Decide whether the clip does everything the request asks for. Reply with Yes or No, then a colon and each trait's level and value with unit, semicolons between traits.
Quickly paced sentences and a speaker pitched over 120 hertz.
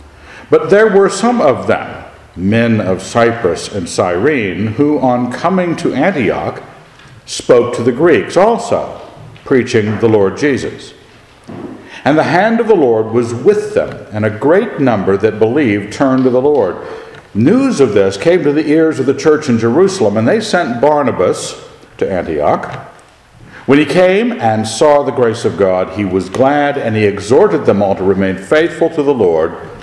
No: average, 170 wpm; low, 135 Hz